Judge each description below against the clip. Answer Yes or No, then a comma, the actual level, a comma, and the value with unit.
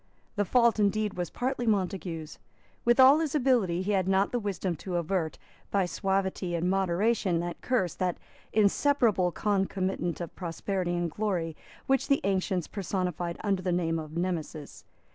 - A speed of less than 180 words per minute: Yes, average, 155 wpm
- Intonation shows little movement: No, average, 3.2 semitones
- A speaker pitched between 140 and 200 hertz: Yes, high, 190 Hz